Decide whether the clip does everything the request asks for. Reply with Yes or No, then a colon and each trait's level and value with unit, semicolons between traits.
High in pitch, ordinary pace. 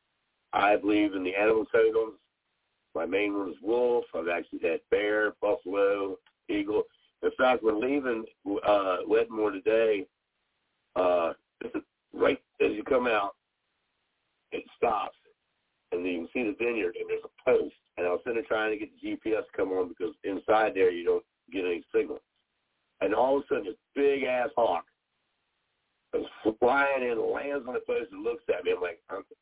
Yes: very high, 365 Hz; average, 175 wpm